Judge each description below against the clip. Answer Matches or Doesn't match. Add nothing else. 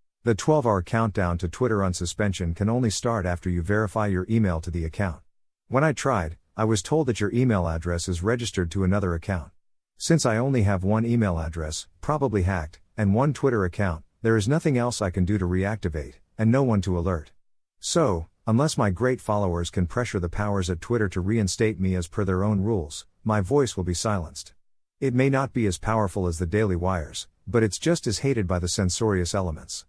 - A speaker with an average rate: Doesn't match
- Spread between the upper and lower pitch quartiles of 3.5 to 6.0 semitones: Matches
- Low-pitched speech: Matches